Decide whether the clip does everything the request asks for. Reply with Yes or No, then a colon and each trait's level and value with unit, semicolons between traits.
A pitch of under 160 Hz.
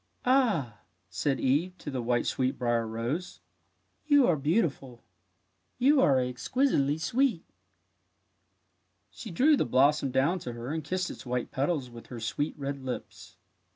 Yes: low, 135 Hz